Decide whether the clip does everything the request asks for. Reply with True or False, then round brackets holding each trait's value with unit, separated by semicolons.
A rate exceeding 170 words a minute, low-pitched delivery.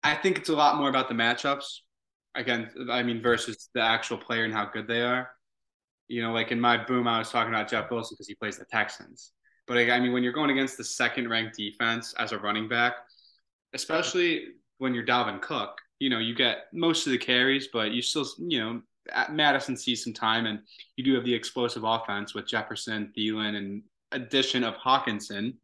True (205 wpm; 120 Hz)